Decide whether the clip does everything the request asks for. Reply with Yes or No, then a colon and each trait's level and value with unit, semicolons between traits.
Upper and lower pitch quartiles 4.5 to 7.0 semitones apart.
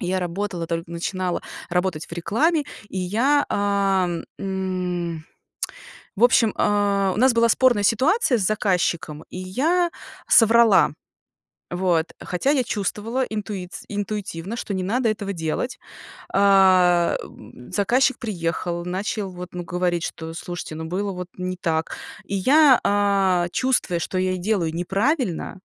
No: average, 3.6 semitones